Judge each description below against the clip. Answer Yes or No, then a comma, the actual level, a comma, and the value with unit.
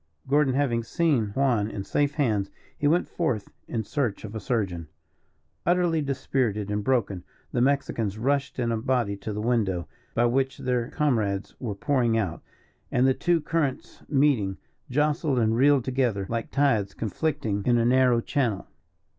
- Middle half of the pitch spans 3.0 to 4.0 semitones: No, average, 4.6 semitones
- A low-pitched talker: Yes, low, 125 Hz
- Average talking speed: Yes, average, 160 wpm